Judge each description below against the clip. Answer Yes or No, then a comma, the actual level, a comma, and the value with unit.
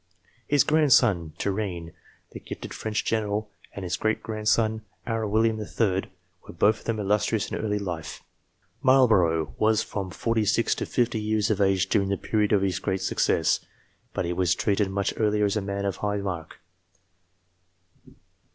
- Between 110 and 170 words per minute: Yes, average, 160 wpm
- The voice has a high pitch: No, low, 105 Hz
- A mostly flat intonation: Yes, narrow, 2.2 semitones